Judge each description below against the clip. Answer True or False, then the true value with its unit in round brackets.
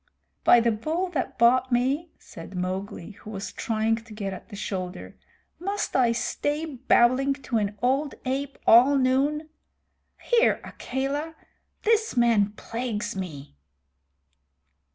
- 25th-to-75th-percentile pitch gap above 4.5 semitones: True (5.0 semitones)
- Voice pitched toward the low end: False (245 Hz)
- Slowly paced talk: True (130 wpm)